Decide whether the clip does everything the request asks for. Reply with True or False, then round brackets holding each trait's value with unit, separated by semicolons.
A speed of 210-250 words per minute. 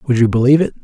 False (285 wpm)